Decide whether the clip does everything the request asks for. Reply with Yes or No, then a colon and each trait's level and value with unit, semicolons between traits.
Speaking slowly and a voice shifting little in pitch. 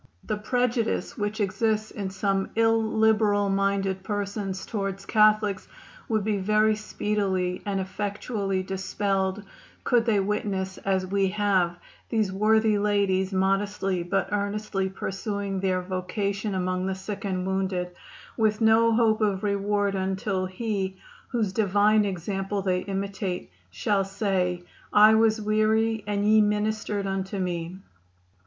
Yes: slow, 125 wpm; narrow, 1.9 semitones